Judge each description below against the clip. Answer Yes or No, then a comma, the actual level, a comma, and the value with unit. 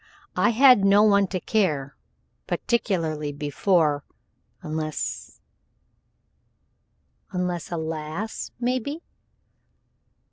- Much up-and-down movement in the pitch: Yes, wide, 5.7 semitones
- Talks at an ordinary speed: No, slow, 80 wpm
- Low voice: No, medium, 180 Hz